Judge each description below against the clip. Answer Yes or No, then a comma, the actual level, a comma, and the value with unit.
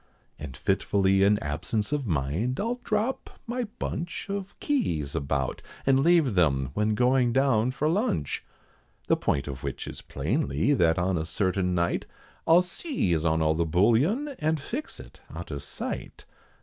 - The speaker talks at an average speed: Yes, average, 160 wpm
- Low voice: Yes, low, 110 Hz